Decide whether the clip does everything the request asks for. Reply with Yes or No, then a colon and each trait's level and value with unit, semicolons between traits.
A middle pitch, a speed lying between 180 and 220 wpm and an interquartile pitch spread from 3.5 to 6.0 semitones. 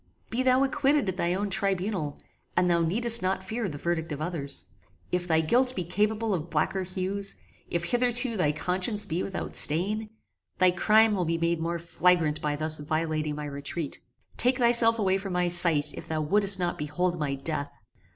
Yes: medium, 180 Hz; average, 185 wpm; average, 4.6 semitones